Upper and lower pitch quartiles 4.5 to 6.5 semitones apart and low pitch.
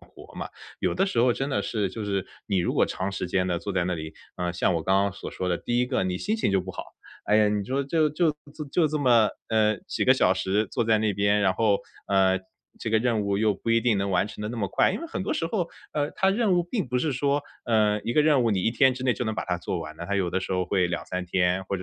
Yes: average, 5.1 semitones; low, 105 Hz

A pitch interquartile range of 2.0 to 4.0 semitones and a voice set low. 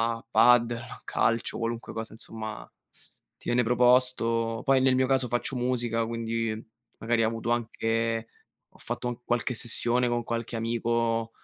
No: narrow, 1.2 semitones; low, 115 Hz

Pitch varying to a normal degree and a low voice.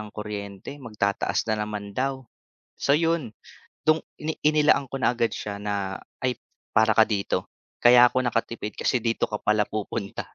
Yes: average, 3.7 semitones; low, 110 Hz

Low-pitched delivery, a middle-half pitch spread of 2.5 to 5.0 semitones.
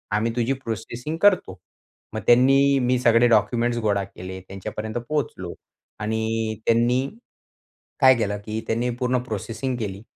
Yes: low, 115 Hz; average, 2.8 semitones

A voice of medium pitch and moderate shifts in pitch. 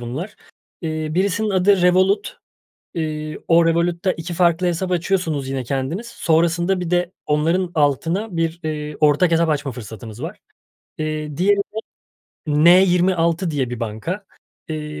Yes: medium, 165 Hz; average, 3.1 semitones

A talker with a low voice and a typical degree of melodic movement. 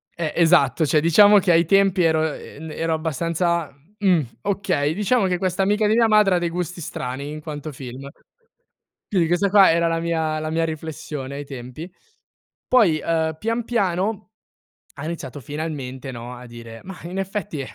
No: medium, 165 Hz; average, 4.3 semitones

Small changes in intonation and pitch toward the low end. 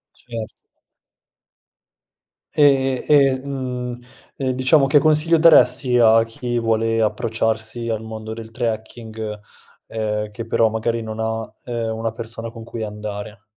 Yes: narrow, 2.3 semitones; low, 115 Hz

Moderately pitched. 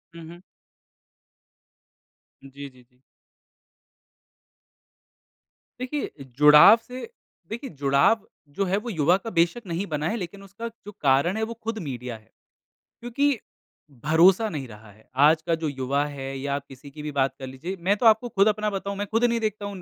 Yes: medium, 170 Hz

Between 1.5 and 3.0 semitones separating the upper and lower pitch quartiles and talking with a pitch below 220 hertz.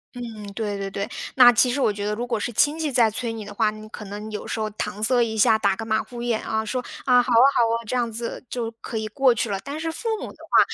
No: narrow, 2.6 semitones; high, 225 Hz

